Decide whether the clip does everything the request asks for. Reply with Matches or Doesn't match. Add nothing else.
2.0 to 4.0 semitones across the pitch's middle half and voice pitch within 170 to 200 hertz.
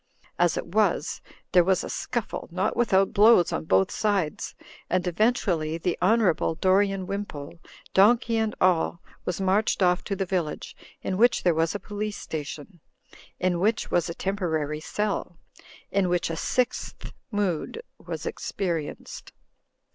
Matches